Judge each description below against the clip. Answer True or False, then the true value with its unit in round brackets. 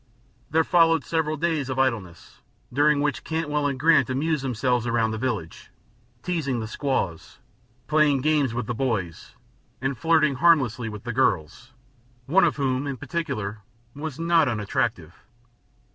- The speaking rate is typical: True (145 wpm)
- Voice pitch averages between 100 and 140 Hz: True (135 Hz)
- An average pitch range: True (5.0 semitones)